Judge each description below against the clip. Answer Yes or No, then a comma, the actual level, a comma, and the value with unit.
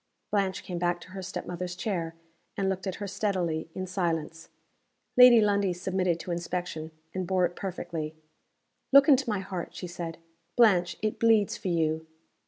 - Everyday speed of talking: Yes, average, 170 wpm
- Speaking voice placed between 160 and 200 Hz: Yes, medium, 185 Hz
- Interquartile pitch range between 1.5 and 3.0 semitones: Yes, narrow, 2.6 semitones